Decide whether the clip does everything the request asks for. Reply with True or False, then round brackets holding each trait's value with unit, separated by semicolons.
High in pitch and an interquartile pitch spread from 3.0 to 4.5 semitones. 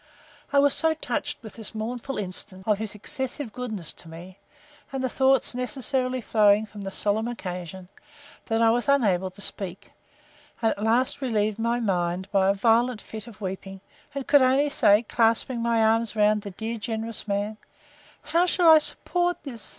True (225 Hz; 3.9 semitones)